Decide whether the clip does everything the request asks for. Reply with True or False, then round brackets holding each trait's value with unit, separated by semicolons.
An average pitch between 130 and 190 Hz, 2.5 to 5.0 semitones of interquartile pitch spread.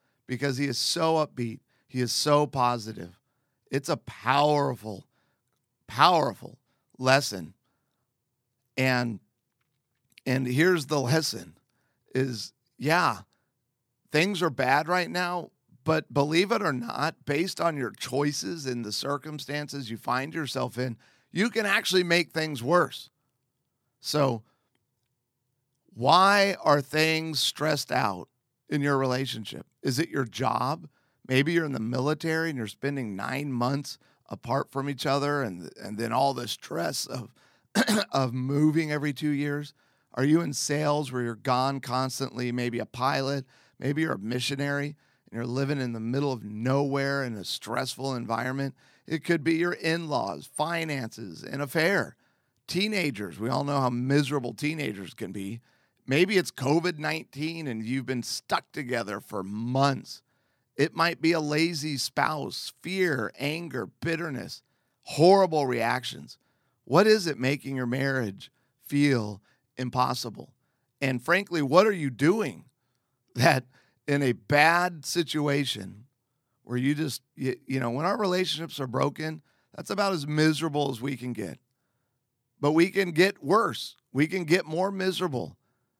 True (140 Hz; 3.5 semitones)